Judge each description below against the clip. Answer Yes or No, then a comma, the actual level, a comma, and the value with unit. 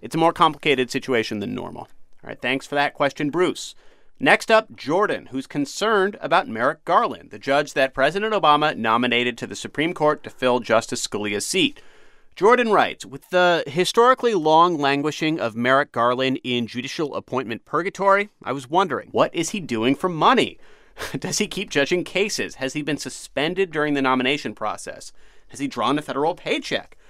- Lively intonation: Yes, wide, 5.9 semitones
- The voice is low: No, medium, 145 Hz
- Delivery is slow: No, average, 175 wpm